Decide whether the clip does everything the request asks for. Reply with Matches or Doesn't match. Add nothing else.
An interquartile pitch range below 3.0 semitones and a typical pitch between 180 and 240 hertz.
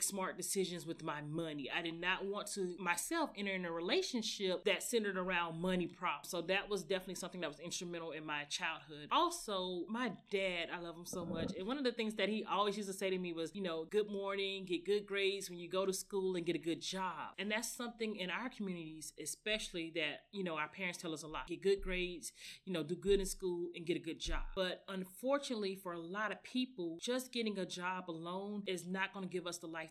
Matches